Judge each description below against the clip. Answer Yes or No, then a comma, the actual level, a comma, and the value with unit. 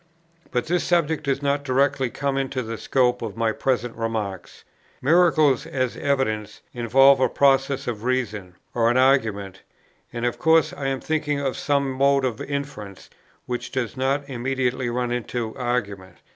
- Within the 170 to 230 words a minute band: No, average, 160 wpm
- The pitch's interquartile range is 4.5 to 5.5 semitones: No, average, 3.0 semitones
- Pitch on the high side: No, low, 130 Hz